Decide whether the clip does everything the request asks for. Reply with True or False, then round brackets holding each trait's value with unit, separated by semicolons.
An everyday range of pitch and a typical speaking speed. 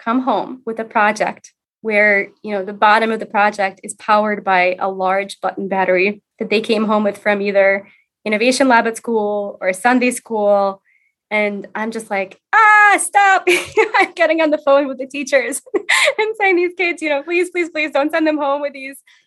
False (6.8 semitones; 195 wpm)